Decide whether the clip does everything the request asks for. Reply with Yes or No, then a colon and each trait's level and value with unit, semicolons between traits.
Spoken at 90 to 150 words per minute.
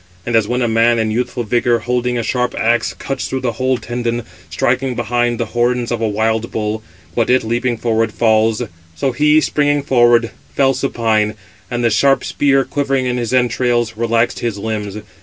No: average, 185 wpm